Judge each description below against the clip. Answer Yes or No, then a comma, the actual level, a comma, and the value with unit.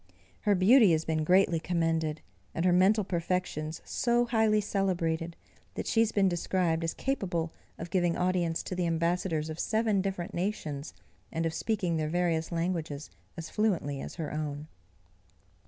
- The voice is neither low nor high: Yes, medium, 175 Hz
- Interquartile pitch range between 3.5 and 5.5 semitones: No, average, 3.1 semitones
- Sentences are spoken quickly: No, average, 155 wpm